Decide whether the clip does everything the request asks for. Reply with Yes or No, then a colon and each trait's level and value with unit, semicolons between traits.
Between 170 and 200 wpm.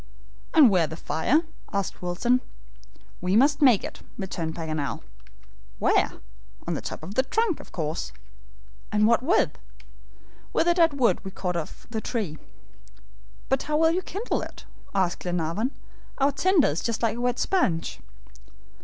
No: average, 155 wpm